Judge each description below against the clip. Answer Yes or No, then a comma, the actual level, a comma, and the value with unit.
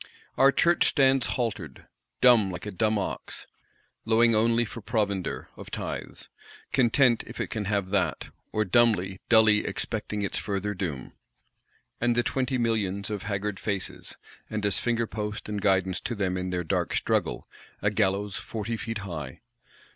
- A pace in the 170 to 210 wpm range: No, average, 155 wpm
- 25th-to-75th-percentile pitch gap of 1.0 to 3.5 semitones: Yes, average, 3.1 semitones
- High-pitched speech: No, low, 105 Hz